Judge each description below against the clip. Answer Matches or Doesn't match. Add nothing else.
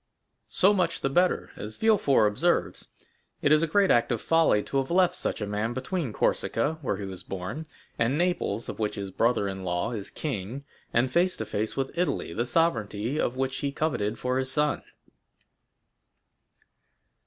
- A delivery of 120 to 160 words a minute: Doesn't match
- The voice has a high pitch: Doesn't match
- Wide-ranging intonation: Matches